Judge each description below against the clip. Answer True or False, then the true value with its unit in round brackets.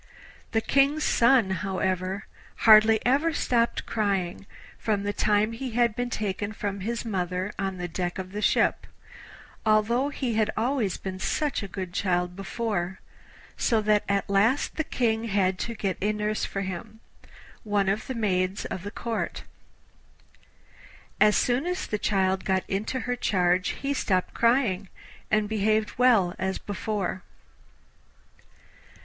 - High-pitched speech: True (210 Hz)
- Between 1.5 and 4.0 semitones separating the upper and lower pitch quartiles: True (3.4 semitones)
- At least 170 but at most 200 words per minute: False (145 wpm)